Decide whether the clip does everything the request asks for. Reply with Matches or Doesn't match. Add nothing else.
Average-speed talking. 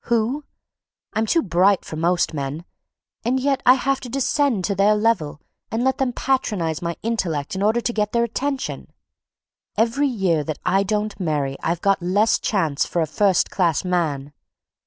Matches